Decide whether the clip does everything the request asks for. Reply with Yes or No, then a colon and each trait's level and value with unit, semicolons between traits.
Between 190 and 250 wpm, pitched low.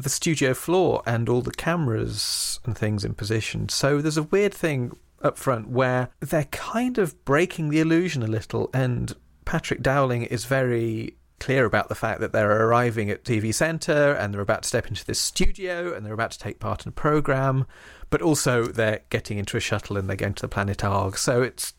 Yes: fast, 205 wpm; low, 125 Hz